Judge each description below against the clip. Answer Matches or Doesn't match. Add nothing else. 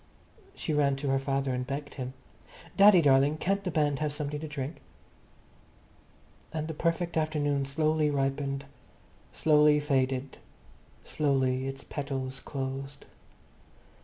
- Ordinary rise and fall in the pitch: Doesn't match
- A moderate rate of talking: Doesn't match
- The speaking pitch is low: Doesn't match